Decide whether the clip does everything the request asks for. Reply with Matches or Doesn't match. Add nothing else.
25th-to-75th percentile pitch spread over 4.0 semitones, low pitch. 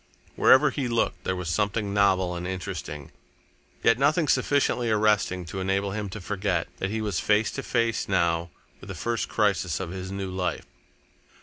Doesn't match